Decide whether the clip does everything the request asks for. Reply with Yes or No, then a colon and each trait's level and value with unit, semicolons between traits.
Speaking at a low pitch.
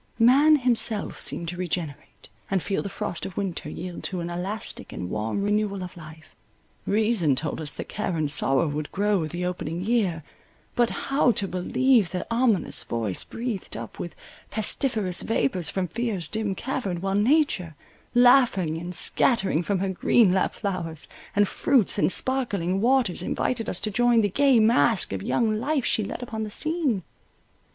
No: high, 195 Hz